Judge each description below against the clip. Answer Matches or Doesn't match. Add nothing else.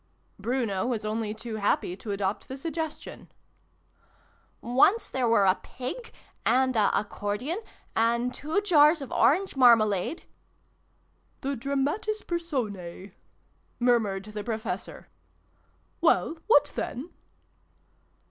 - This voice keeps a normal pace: Doesn't match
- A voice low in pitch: Doesn't match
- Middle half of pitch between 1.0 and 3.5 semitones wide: Doesn't match